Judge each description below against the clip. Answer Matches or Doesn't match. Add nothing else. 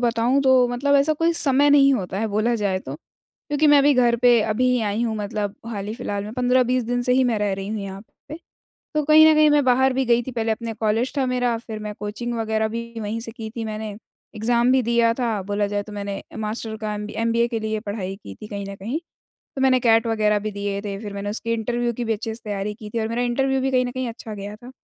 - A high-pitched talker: Matches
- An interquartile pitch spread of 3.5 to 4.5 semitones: Doesn't match